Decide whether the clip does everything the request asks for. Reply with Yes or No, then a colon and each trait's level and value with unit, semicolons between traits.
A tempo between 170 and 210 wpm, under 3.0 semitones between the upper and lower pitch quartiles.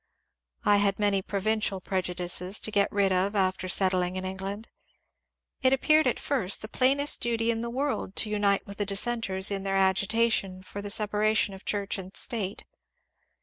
Yes: average, 175 wpm; narrow, 2.6 semitones